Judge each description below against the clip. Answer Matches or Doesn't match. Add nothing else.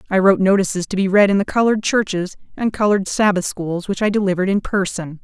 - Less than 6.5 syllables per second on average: Doesn't match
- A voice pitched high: Matches